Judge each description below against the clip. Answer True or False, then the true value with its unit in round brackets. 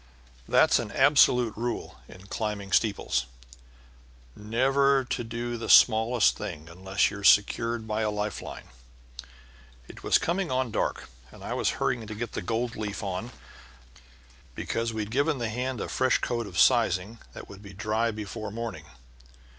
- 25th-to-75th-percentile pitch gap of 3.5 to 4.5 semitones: False (2.8 semitones)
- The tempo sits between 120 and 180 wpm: True (155 wpm)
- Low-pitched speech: True (110 Hz)